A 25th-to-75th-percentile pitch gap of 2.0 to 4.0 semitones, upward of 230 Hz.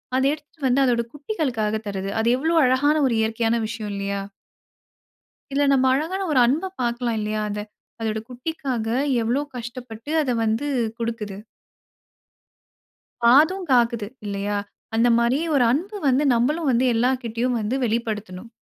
Yes: average, 3.7 semitones; high, 240 Hz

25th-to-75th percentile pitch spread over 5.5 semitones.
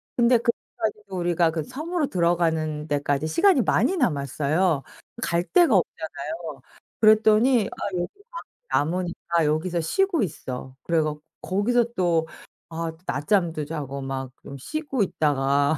Yes: wide, 6.3 semitones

